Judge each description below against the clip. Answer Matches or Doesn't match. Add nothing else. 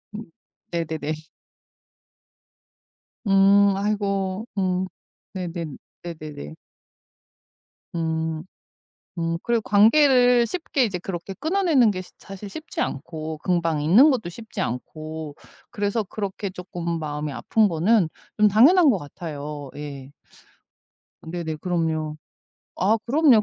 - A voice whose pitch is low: Doesn't match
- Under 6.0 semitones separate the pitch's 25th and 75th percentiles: Matches